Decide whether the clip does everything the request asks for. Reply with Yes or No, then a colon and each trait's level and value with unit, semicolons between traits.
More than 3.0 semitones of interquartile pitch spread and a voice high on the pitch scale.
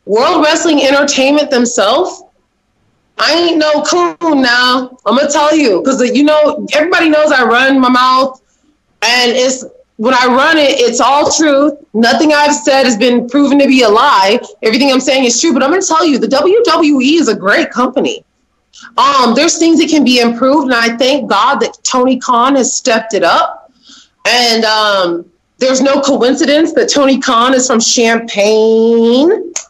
Yes: average, 3.7 semitones; very high, 265 Hz